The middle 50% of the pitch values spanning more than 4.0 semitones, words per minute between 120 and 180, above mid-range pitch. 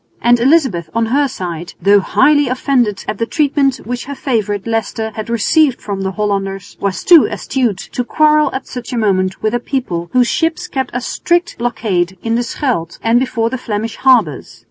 No: average, 4.8 semitones; average, 190 wpm; high, 235 Hz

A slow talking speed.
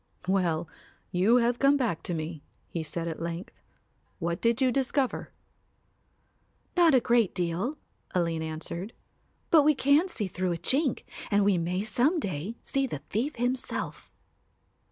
No: average, 150 wpm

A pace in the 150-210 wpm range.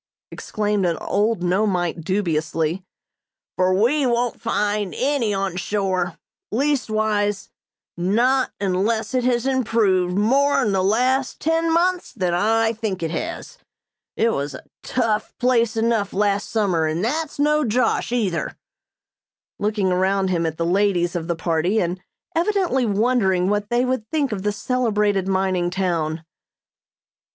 No: average, 140 wpm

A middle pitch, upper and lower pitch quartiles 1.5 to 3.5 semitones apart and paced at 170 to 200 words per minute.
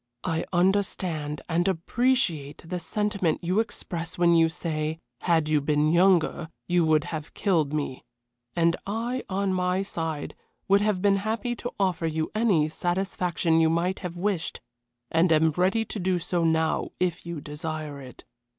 No: medium, 175 Hz; average, 3.1 semitones; average, 160 wpm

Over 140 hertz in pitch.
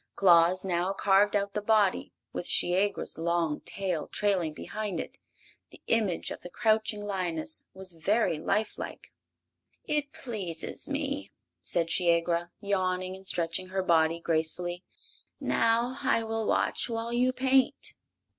Yes: high, 190 Hz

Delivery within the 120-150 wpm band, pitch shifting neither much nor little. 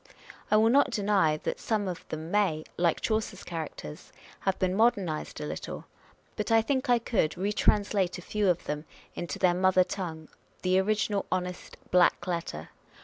No: average, 165 wpm; average, 3.8 semitones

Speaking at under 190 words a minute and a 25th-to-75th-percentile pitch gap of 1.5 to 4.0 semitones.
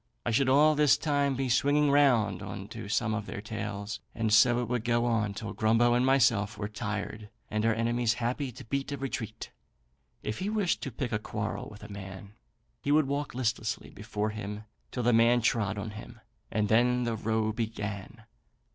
No: average, 195 wpm; average, 2.8 semitones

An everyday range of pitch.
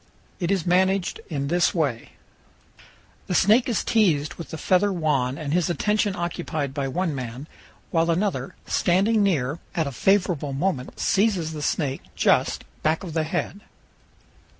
Yes: average, 4.6 semitones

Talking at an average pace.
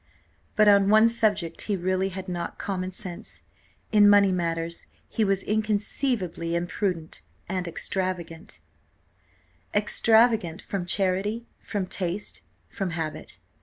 No: slow, 115 wpm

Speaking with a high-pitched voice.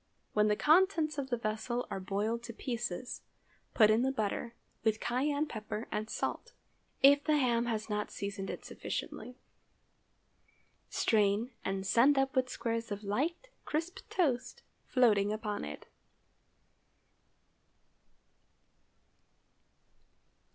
Yes: high, 235 Hz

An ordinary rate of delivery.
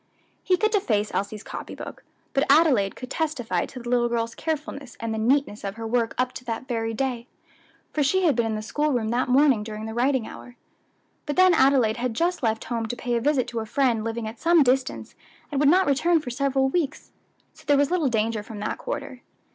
No: fast, 225 wpm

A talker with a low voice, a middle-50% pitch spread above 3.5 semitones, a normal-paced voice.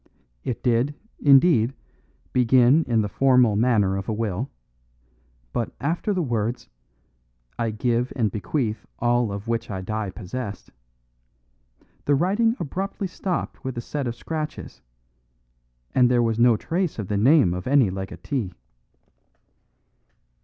No: low, 120 Hz; average, 4.3 semitones; slow, 130 wpm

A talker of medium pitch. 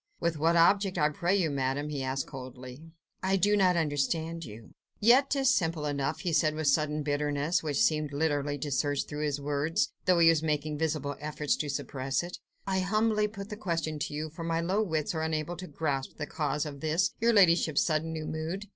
Yes: medium, 155 Hz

